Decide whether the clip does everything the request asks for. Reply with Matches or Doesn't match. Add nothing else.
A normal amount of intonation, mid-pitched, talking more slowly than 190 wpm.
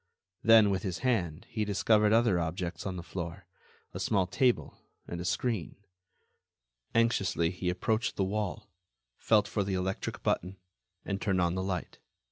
Doesn't match